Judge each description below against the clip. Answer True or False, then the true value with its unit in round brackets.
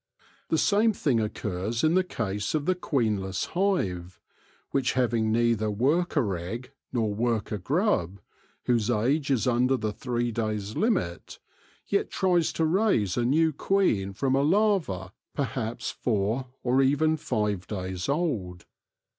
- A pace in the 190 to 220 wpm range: False (140 wpm)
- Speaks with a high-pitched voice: False (120 Hz)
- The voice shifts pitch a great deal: True (6.9 semitones)